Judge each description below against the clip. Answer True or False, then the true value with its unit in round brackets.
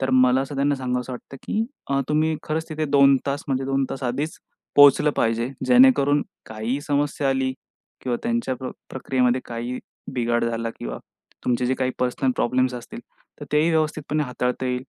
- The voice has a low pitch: True (130 Hz)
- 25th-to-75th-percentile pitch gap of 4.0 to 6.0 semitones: False (2.7 semitones)